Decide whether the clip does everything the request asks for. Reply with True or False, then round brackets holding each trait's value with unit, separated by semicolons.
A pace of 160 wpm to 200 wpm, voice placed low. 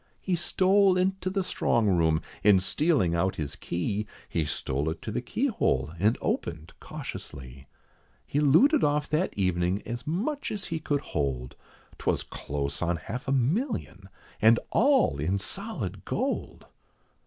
False (145 wpm; 105 Hz)